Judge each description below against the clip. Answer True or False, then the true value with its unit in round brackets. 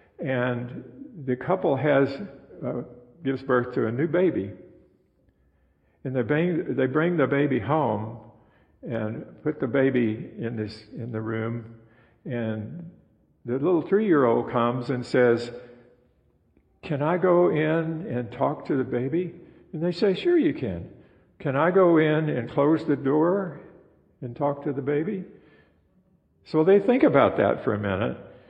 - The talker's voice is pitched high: False (135 Hz)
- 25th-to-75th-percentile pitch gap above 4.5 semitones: True (5.5 semitones)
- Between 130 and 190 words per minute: True (150 wpm)